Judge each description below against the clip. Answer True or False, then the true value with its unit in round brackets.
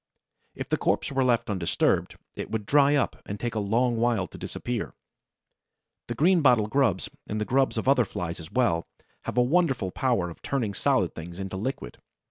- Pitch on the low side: True (120 Hz)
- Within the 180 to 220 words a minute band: True (185 wpm)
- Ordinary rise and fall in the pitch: True (5.0 semitones)